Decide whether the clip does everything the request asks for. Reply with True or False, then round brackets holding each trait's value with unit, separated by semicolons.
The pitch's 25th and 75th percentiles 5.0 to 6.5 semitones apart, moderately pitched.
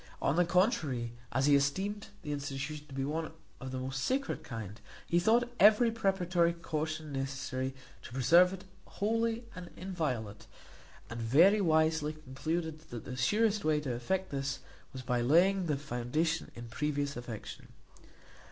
True (5.3 semitones; 155 Hz)